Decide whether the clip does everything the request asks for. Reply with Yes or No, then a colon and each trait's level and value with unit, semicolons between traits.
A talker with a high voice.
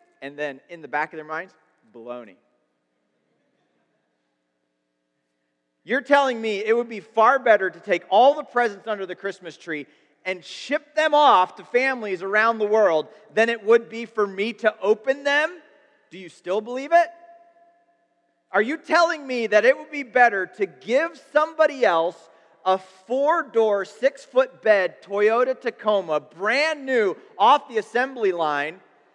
Yes: high, 215 Hz